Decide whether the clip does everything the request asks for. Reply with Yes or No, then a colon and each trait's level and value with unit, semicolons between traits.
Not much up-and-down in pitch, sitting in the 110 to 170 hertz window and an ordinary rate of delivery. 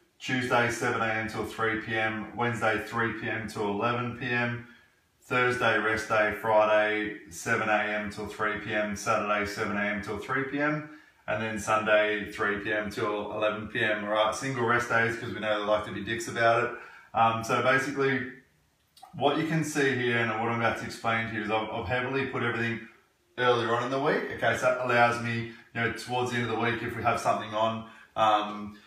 Yes: narrow, 2.0 semitones; low, 115 Hz; average, 195 wpm